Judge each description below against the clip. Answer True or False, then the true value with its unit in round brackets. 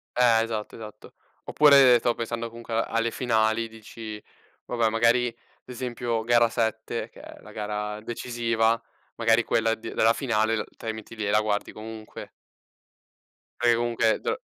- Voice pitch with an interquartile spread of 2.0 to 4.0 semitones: False (1.3 semitones)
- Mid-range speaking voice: False (115 Hz)